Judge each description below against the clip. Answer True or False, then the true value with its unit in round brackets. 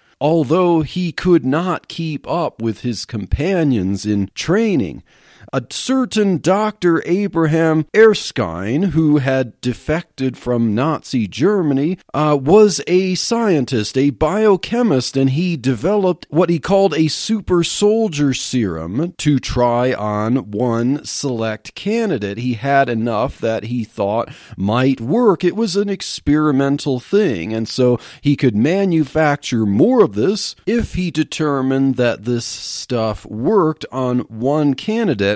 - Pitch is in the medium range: True (145 Hz)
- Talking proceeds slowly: True (125 wpm)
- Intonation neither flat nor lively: False (6.4 semitones)